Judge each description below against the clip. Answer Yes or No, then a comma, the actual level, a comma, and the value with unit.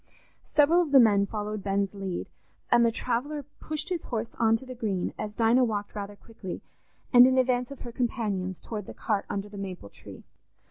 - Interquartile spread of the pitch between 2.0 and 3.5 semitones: No, average, 3.9 semitones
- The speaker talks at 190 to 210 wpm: Yes, average, 195 wpm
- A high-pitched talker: Yes, high, 225 Hz